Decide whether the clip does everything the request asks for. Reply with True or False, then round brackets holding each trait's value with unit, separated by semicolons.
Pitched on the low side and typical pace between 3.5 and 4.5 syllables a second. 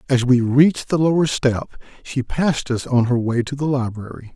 False (130 Hz; 5.2 syllables/s)